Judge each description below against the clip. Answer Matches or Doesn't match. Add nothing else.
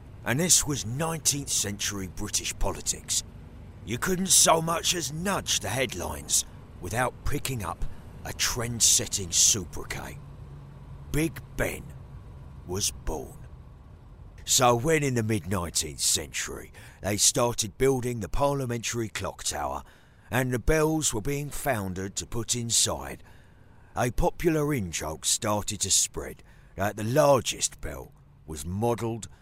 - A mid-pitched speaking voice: Doesn't match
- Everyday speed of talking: Doesn't match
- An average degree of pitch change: Doesn't match